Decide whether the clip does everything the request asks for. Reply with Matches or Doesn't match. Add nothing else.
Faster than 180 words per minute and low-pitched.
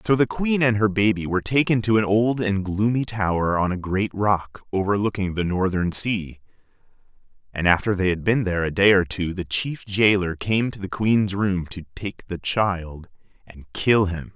Matches